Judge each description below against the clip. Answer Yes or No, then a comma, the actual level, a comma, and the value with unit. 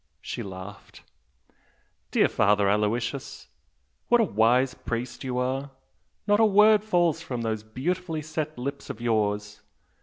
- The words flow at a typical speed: No, slow, 130 wpm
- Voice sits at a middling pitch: No, low, 125 Hz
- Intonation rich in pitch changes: Yes, wide, 6.7 semitones